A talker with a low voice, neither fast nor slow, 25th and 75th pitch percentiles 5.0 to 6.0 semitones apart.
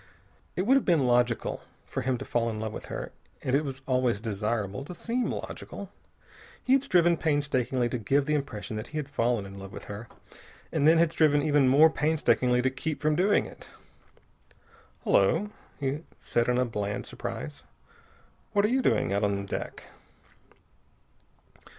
Yes: low, 130 Hz; average, 170 wpm; wide, 5.6 semitones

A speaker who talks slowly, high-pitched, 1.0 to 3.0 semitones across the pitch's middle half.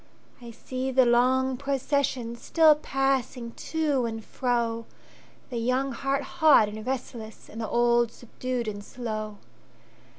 Yes: slow, 110 wpm; high, 245 Hz; narrow, 2.6 semitones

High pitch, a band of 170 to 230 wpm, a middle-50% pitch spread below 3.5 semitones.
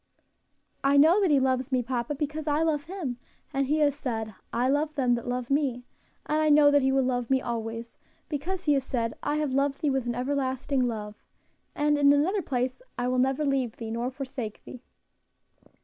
Yes: very high, 270 Hz; fast, 205 wpm; average, 3.0 semitones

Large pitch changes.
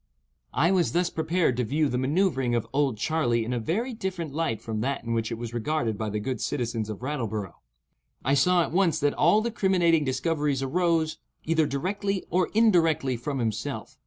Yes: wide, 6.1 semitones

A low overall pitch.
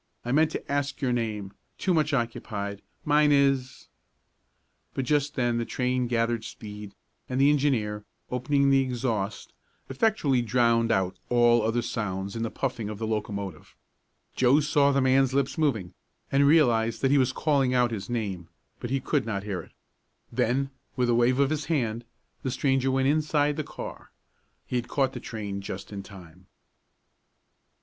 Yes: low, 125 Hz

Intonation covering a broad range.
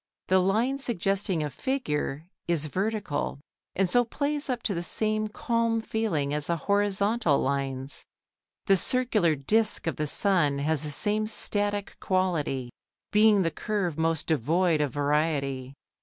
Yes: wide, 6.4 semitones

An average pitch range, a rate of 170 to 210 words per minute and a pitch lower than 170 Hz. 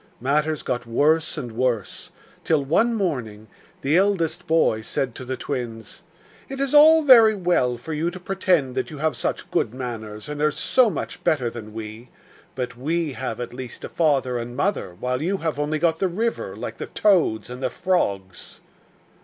No: wide, 6.1 semitones; average, 185 wpm; medium, 140 Hz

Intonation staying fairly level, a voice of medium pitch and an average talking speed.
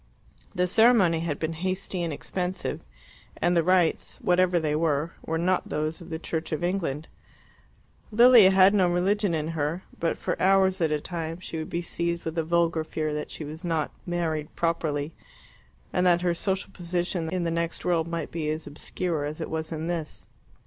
Yes: narrow, 2.2 semitones; medium, 170 Hz; average, 190 wpm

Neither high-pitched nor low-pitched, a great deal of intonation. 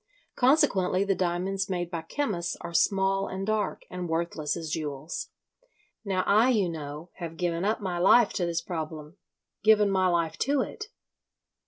No: medium, 180 Hz; average, 3.0 semitones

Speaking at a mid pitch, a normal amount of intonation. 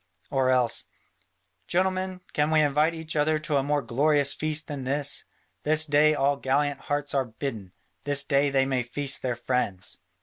No: medium, 145 Hz; narrow, 2.3 semitones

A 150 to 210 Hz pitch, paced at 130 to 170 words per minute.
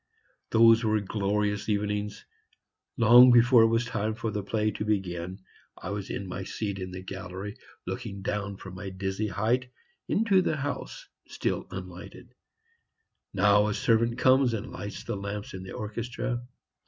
No: low, 105 Hz; average, 155 wpm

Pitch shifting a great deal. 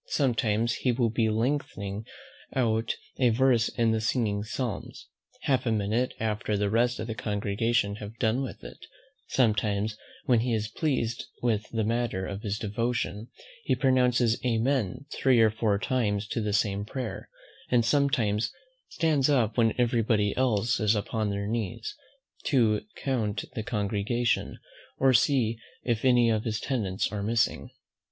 No: average, 2.7 semitones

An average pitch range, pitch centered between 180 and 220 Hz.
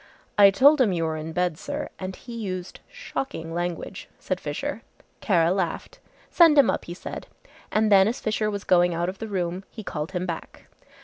Yes: average, 3.8 semitones; medium, 185 Hz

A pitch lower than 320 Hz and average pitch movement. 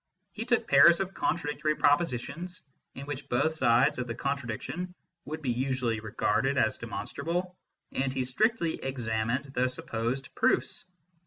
Yes: low, 135 Hz; average, 4.2 semitones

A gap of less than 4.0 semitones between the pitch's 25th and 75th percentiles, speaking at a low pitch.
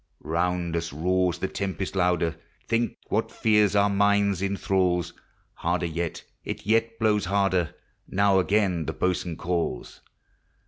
Yes: average, 2.8 semitones; very low, 95 Hz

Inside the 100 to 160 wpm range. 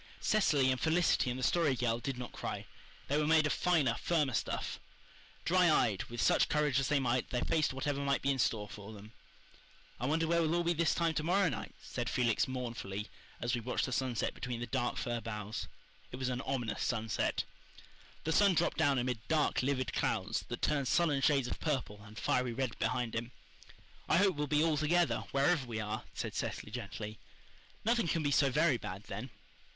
No: fast, 205 wpm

